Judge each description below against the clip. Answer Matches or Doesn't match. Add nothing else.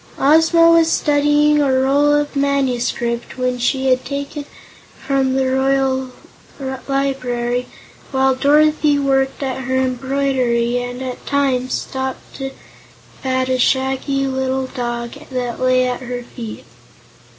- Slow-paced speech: Matches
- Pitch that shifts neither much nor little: Doesn't match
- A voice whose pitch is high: Matches